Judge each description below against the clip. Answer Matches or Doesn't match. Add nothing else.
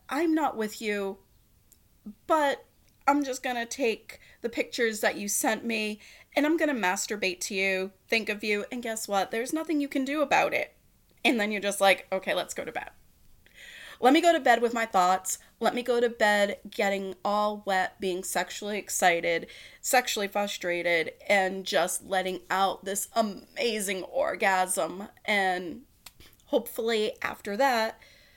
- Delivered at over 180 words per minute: Doesn't match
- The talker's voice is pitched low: Doesn't match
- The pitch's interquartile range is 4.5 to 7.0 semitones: Doesn't match